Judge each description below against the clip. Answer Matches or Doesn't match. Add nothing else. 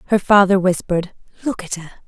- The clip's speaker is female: Matches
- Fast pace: Doesn't match